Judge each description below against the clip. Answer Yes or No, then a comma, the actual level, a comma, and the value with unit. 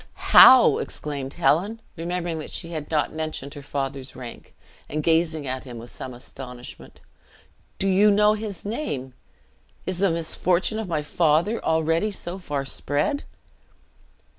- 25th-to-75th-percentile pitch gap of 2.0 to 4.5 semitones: No, average, 5.0 semitones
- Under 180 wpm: Yes, average, 140 wpm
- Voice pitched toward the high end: No, medium, 160 Hz